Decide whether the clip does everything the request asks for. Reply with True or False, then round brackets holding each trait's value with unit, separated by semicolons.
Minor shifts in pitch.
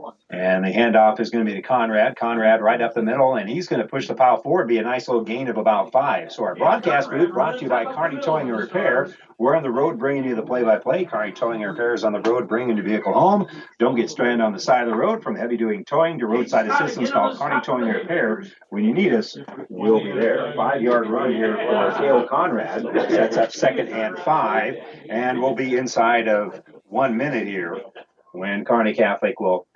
True (2.3 semitones)